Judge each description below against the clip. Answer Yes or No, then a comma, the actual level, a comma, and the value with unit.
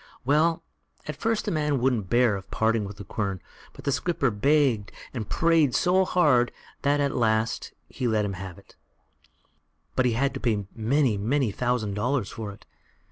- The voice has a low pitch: Yes, low, 125 Hz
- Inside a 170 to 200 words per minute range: Yes, average, 180 wpm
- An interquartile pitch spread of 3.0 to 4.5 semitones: No, average, 5.3 semitones